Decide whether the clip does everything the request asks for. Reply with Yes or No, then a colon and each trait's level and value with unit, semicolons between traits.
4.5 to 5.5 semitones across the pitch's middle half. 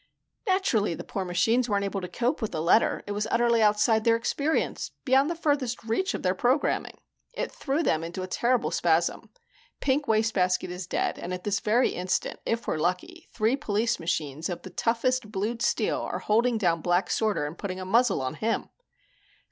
Yes: average, 5.0 semitones